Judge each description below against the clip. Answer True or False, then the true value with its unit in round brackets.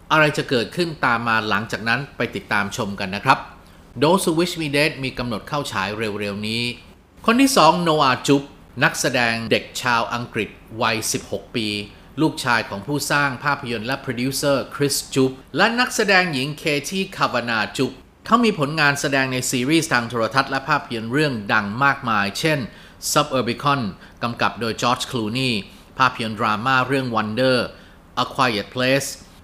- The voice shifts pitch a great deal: False (4.5 semitones)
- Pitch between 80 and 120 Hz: False (130 Hz)